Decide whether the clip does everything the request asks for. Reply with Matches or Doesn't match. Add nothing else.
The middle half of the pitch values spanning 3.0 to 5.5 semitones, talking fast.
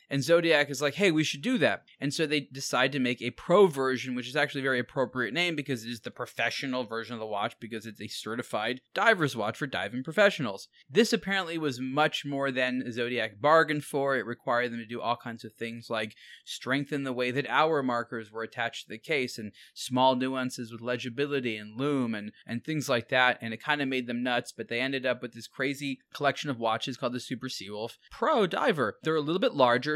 Matches